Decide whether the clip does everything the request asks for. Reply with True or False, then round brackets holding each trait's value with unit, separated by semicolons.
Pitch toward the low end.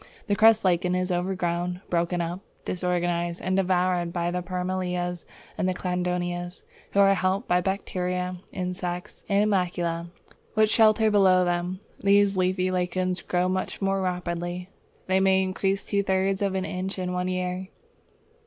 False (180 Hz)